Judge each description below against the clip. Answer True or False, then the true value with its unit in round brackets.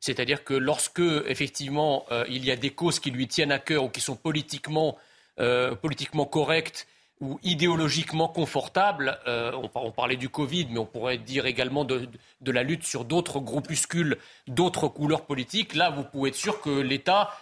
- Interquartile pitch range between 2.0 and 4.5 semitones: True (3.4 semitones)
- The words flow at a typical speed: True (180 wpm)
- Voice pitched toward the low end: False (145 Hz)